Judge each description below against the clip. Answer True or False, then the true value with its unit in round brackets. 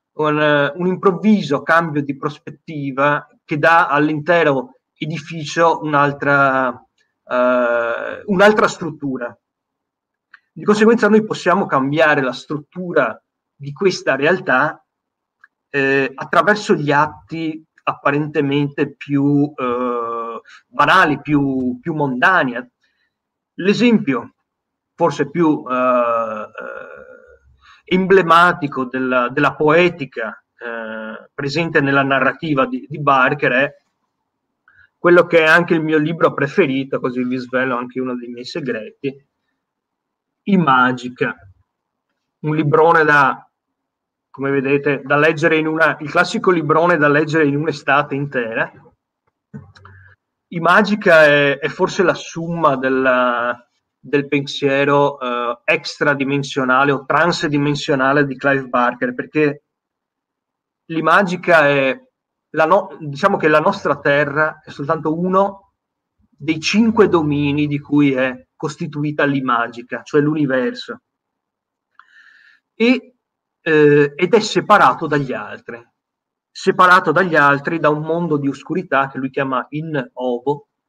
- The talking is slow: True (110 wpm)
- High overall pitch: False (150 Hz)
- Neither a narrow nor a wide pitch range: True (3.6 semitones)